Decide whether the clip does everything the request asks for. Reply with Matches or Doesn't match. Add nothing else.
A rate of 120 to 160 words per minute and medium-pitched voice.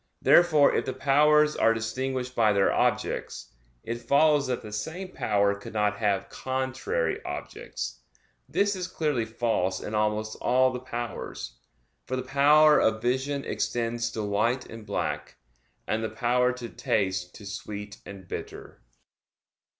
Doesn't match